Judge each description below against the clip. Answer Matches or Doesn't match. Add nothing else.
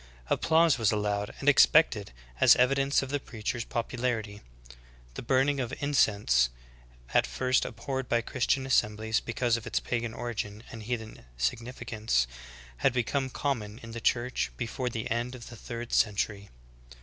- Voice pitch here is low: Matches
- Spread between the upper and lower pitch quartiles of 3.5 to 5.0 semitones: Doesn't match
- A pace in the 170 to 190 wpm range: Doesn't match